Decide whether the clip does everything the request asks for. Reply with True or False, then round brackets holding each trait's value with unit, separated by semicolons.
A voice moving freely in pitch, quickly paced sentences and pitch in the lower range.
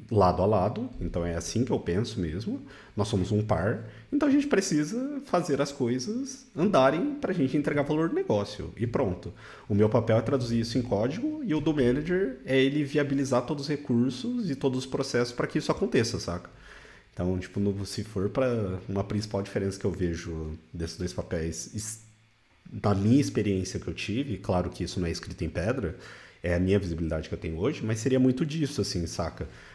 True (6.8 semitones; 200 wpm; 110 Hz)